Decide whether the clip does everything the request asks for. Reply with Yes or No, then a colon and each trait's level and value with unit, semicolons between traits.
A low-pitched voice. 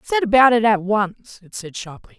No: medium, 185 Hz